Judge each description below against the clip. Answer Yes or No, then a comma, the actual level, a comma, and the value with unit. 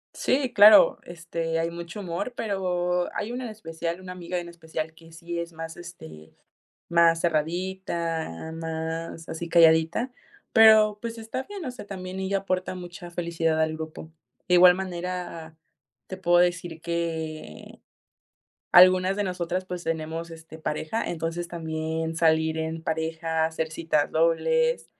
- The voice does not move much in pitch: Yes, narrow, 2.1 semitones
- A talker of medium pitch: Yes, medium, 170 Hz